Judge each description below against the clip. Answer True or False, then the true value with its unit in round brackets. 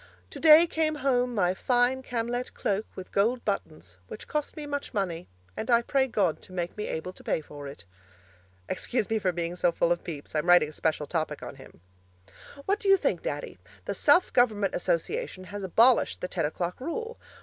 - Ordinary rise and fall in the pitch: False (7.1 semitones)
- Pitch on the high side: True (205 Hz)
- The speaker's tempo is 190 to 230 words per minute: True (195 wpm)